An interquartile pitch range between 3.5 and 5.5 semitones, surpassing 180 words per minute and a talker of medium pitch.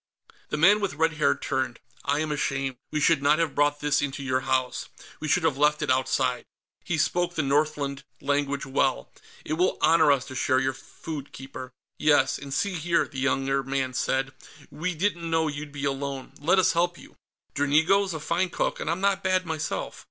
No: average, 3.1 semitones; average, 195 wpm; medium, 145 Hz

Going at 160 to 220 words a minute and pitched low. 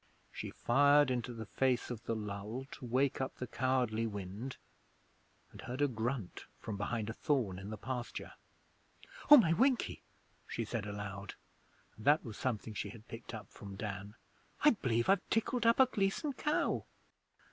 Yes: average, 170 wpm; low, 120 Hz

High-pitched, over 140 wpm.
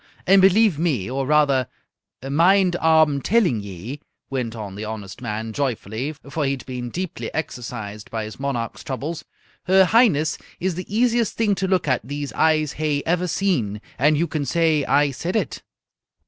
No: medium, 145 Hz; average, 170 wpm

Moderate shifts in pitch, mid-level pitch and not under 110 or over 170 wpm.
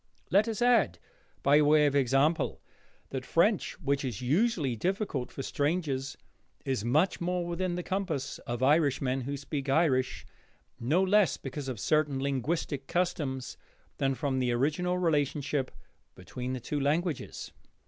Yes: average, 4.6 semitones; medium, 145 Hz; average, 140 wpm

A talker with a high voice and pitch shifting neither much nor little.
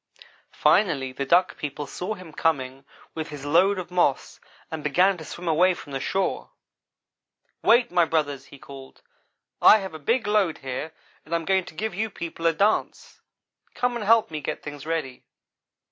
No: medium, 165 Hz; average, 4.8 semitones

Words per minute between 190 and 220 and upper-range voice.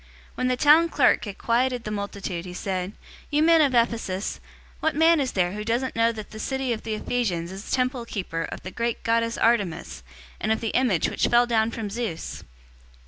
Yes: fast, 205 wpm; high, 230 Hz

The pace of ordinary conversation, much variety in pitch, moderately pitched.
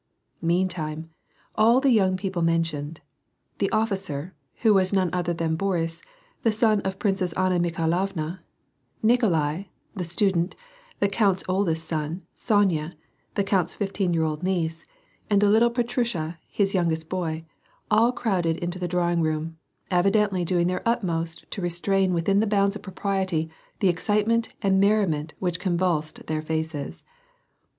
No: average, 145 wpm; average, 3.4 semitones; medium, 180 Hz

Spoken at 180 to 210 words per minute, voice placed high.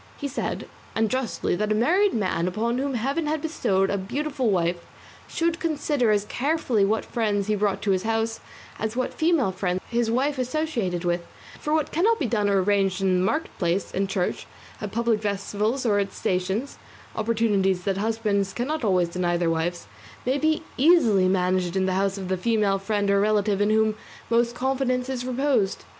Yes: average, 185 wpm; high, 215 Hz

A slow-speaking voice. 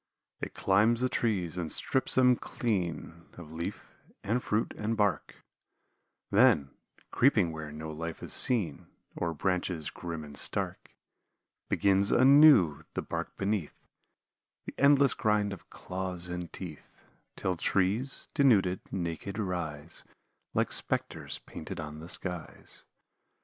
Yes: slow, 125 wpm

